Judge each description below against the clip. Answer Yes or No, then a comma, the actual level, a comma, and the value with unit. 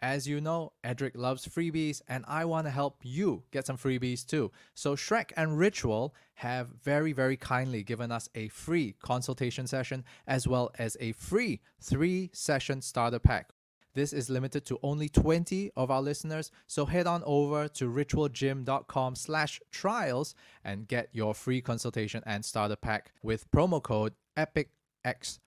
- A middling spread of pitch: Yes, average, 3.8 semitones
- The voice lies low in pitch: Yes, low, 130 Hz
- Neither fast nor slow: Yes, average, 160 wpm